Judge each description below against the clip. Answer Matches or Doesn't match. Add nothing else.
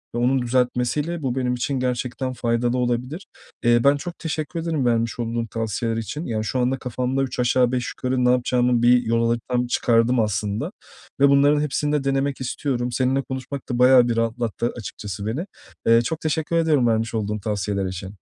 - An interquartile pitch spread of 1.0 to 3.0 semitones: Matches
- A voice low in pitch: Matches